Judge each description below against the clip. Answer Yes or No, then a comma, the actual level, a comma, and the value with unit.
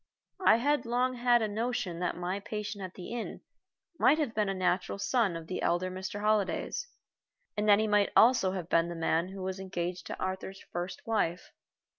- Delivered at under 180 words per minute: No, average, 195 wpm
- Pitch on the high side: Yes, high, 195 Hz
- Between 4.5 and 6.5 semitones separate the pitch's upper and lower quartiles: No, average, 3.7 semitones